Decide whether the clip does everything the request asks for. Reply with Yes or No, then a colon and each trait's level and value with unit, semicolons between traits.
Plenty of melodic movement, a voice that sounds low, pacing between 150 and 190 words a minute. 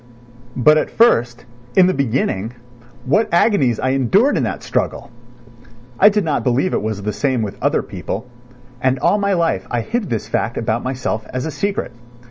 Yes: wide, 8.0 semitones; low, 130 Hz; average, 180 wpm